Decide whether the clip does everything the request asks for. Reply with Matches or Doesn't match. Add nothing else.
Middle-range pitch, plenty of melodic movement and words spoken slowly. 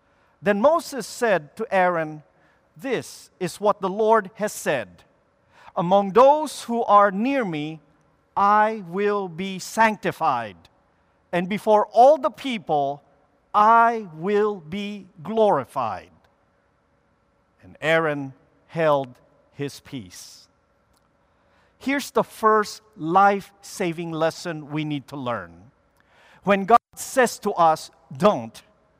Matches